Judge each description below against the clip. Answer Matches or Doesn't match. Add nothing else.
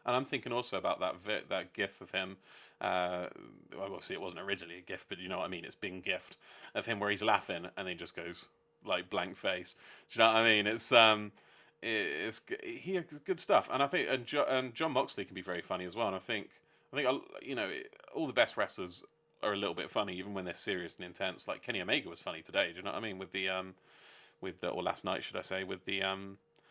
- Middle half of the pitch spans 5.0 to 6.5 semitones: Matches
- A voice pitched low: Matches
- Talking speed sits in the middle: Doesn't match